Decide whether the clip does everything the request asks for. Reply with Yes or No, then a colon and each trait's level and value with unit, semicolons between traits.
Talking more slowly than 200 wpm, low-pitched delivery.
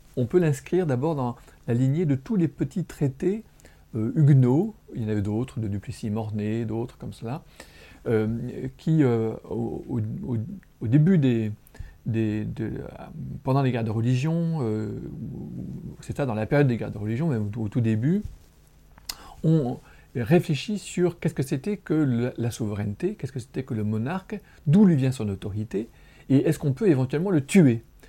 Yes: average, 170 wpm; low, 130 Hz